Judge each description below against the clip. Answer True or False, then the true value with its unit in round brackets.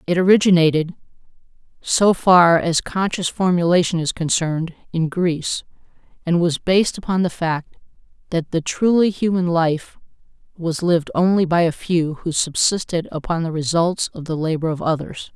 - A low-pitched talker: False (170 Hz)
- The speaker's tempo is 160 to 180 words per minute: False (150 wpm)